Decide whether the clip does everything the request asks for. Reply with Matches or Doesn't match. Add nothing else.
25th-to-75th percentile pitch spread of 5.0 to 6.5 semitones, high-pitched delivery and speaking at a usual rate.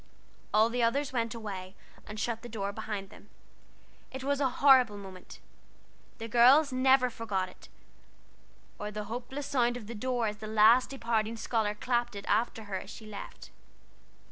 Doesn't match